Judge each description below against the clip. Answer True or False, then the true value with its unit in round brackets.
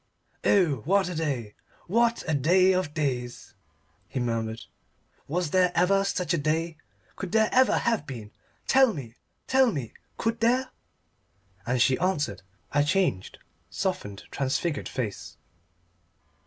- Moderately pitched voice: True (160 Hz)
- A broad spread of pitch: True (7.1 semitones)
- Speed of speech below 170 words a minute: True (140 wpm)